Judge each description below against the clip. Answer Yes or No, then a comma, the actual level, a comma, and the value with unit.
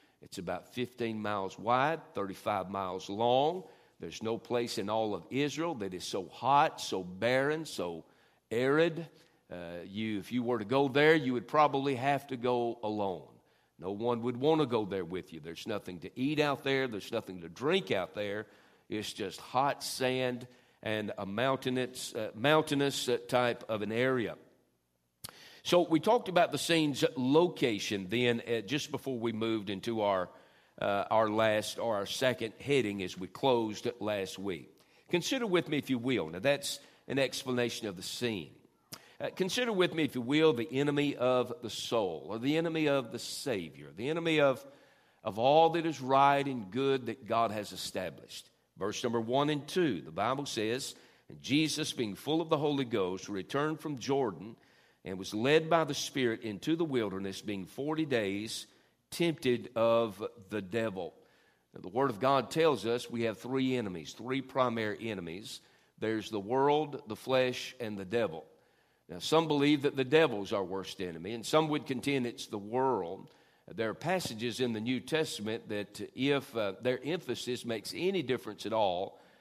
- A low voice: Yes, low, 125 Hz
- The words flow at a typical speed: Yes, average, 175 wpm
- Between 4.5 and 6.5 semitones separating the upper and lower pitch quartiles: Yes, average, 5.0 semitones